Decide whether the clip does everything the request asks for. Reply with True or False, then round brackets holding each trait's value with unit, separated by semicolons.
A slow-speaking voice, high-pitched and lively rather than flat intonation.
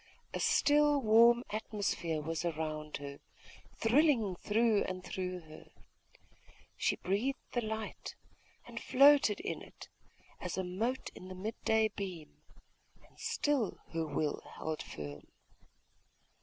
True (125 wpm; 200 Hz; 6.1 semitones)